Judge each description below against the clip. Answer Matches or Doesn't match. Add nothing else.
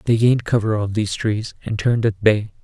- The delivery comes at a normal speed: Doesn't match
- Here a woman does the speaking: Doesn't match